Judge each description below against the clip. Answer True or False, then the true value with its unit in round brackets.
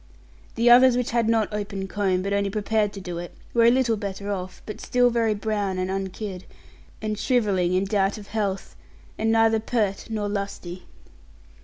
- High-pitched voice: True (205 Hz)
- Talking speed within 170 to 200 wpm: True (180 wpm)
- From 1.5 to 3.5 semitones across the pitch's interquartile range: True (2.5 semitones)